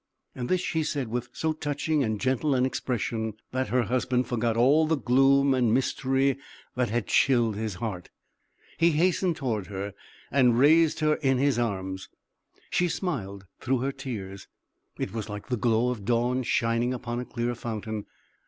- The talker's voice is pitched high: No, low, 125 Hz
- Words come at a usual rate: Yes, average, 165 wpm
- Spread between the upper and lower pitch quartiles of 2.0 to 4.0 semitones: Yes, average, 3.5 semitones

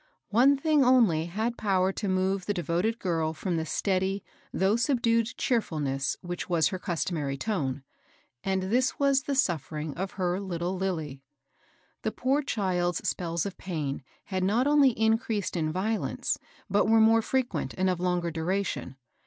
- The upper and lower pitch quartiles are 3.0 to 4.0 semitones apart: No, average, 4.7 semitones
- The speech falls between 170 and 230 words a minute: No, average, 160 wpm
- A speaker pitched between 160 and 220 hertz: Yes, high, 190 Hz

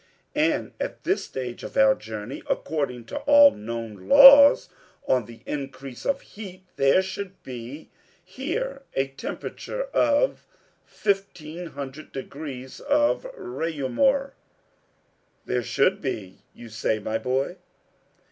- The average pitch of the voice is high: No, medium, 140 Hz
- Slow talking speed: Yes, slow, 120 wpm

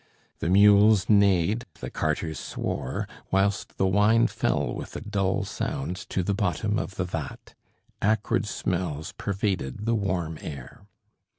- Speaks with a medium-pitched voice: No, very low, 95 Hz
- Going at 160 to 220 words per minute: No, slow, 135 wpm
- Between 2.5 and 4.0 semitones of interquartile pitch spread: Yes, average, 3.1 semitones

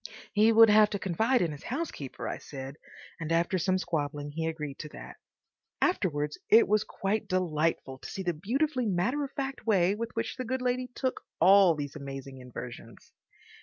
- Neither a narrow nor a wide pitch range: No, wide, 7.2 semitones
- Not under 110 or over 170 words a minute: No, average, 180 wpm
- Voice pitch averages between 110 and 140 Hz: No, medium, 185 Hz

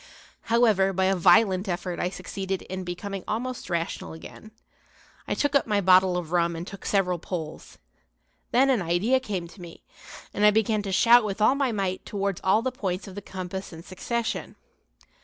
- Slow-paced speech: No, average, 185 wpm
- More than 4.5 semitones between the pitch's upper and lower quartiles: No, average, 3.2 semitones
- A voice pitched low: No, high, 195 Hz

